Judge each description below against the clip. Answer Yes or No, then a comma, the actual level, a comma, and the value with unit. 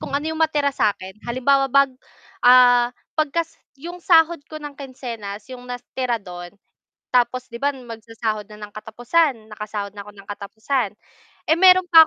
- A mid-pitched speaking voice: No, high, 245 Hz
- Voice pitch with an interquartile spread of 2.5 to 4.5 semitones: No, average, 5.0 semitones